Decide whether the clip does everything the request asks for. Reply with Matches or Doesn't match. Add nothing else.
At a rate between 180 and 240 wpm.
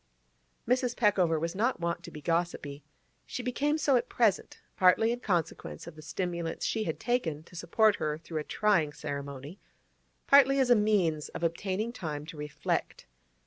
Doesn't match